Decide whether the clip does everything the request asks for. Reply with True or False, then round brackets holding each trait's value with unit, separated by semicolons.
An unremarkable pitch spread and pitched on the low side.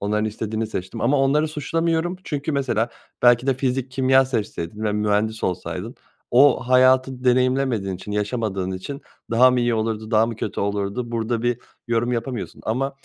True (3.6 semitones; 120 Hz)